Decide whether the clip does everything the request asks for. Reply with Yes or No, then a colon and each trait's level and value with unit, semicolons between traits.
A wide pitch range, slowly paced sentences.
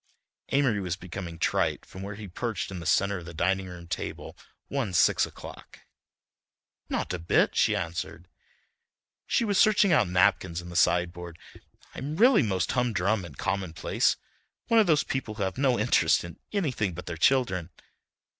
No: wide, 6.1 semitones; average, 165 wpm